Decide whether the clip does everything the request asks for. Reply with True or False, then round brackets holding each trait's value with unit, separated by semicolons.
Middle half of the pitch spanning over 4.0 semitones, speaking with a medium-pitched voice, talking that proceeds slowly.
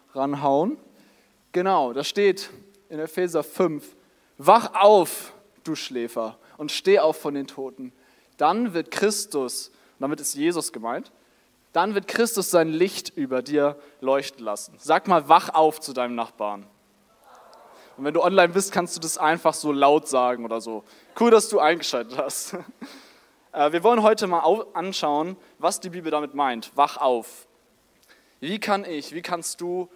False (5.0 semitones; 160 Hz; 155 wpm)